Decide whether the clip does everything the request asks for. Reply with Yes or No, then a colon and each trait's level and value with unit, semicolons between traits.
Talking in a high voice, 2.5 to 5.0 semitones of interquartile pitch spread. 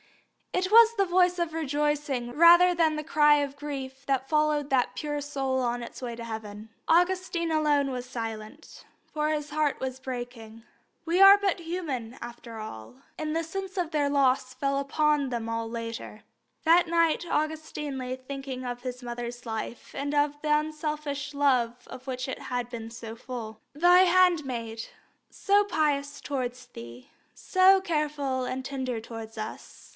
Yes: very high, 280 Hz; average, 4.2 semitones